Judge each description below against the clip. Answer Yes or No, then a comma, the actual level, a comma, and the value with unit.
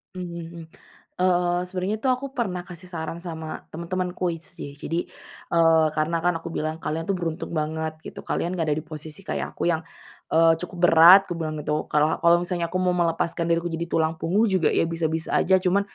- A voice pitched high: No, medium, 170 Hz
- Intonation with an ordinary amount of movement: No, narrow, 2.0 semitones